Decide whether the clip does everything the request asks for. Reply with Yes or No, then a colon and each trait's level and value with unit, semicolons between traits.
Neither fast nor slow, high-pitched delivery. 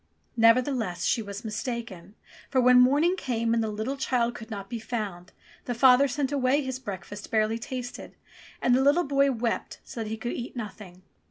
Yes: average, 190 wpm; high, 235 Hz